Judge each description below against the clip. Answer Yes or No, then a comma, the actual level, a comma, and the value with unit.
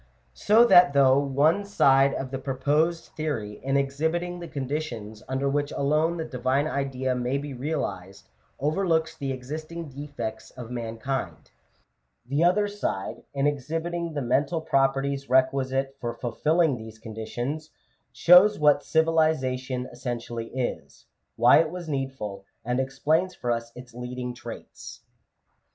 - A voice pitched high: No, low, 135 Hz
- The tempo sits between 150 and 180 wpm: No, slow, 135 wpm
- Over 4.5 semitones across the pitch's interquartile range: No, average, 3.9 semitones